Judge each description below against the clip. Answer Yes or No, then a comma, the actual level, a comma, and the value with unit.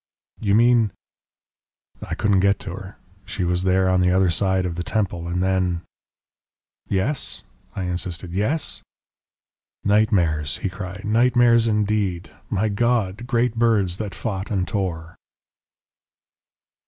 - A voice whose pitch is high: No, very low, 95 Hz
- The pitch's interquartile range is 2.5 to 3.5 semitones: Yes, average, 3.1 semitones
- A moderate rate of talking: No, slow, 130 wpm